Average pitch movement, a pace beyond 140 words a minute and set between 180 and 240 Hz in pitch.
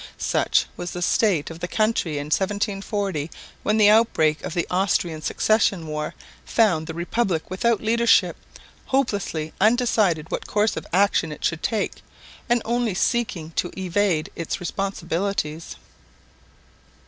No: average, 4.8 semitones; slow, 135 wpm; high, 190 Hz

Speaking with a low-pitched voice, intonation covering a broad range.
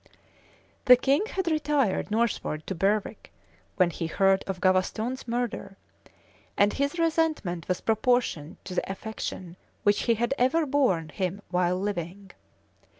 No: high, 205 Hz; wide, 5.8 semitones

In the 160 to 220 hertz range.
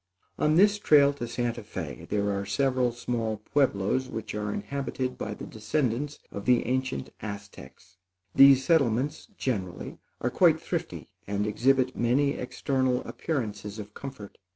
No: low, 125 Hz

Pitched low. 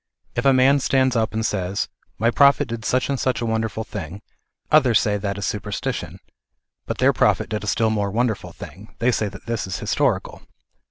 Yes: low, 110 Hz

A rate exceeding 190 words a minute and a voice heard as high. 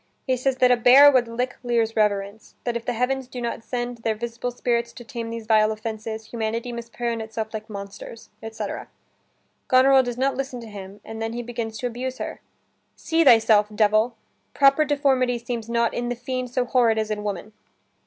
Yes: average, 200 wpm; high, 235 Hz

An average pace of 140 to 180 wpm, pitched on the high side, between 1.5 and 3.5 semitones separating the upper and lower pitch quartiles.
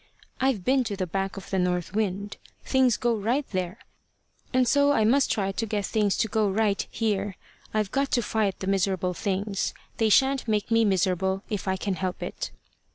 No: average, 195 wpm; high, 205 Hz; average, 3.1 semitones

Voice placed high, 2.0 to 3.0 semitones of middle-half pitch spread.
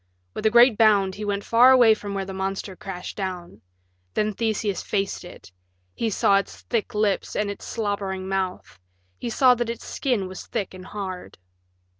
Yes: high, 200 Hz; narrow, 2.5 semitones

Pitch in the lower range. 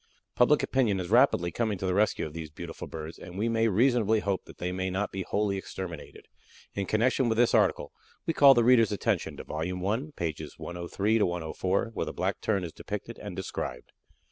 Yes: low, 100 Hz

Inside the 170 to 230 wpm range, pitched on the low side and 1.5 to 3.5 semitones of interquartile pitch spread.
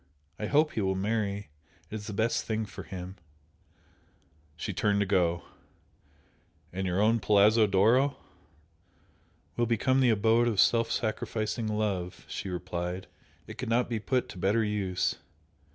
No: average, 150 wpm; low, 105 Hz; average, 3.2 semitones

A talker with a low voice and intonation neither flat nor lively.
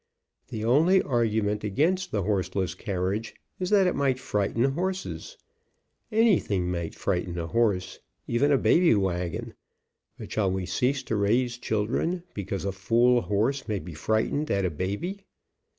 No: low, 110 Hz; wide, 6.3 semitones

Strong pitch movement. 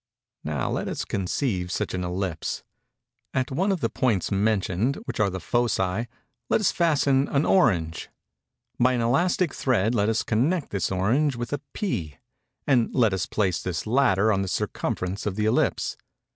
Yes: wide, 6.0 semitones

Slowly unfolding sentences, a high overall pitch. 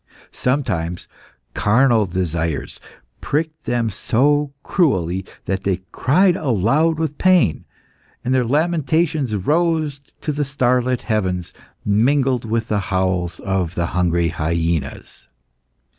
No: slow, 110 wpm; low, 115 Hz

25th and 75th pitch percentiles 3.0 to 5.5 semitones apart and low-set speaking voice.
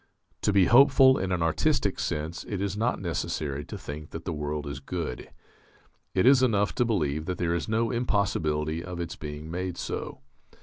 Yes: average, 5.1 semitones; very low, 85 Hz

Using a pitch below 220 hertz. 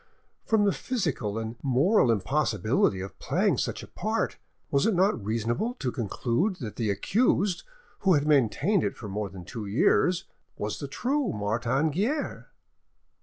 Yes: low, 135 Hz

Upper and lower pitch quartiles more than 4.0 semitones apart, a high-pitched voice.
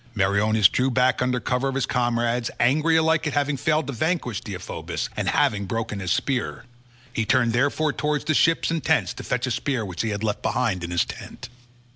No: average, 4.7 semitones; low, 125 Hz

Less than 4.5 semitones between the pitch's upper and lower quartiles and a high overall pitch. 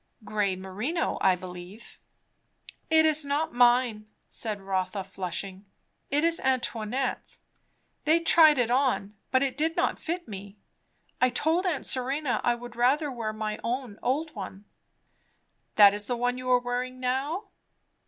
No: average, 5.3 semitones; high, 245 Hz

